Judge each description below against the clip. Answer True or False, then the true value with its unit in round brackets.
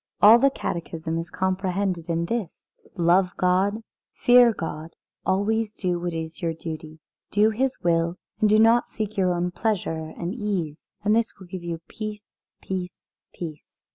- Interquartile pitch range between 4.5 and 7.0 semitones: False (4.1 semitones)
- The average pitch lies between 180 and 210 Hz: True (185 Hz)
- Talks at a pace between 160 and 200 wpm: True (165 wpm)